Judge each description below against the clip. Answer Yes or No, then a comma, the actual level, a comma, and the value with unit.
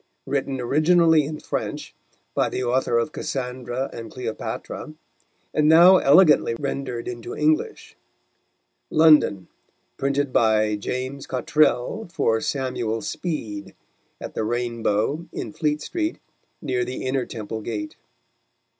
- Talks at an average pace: No, slow, 115 wpm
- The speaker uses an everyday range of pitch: Yes, average, 4.5 semitones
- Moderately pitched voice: No, low, 130 Hz